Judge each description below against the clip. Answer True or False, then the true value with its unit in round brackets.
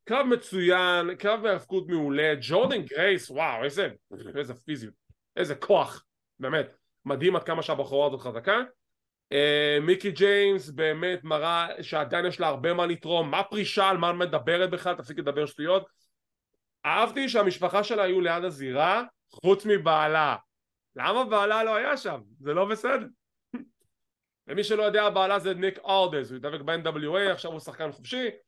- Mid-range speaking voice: True (180 Hz)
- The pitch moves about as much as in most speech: True (4.6 semitones)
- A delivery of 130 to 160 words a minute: True (150 wpm)